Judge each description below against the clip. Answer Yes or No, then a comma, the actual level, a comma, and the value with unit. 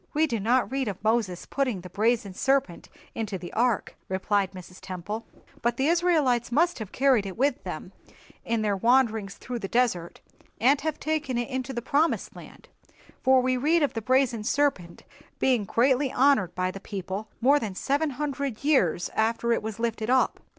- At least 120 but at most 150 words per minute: No, average, 180 wpm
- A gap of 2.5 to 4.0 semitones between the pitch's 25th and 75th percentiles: No, average, 4.8 semitones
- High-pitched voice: Yes, high, 235 Hz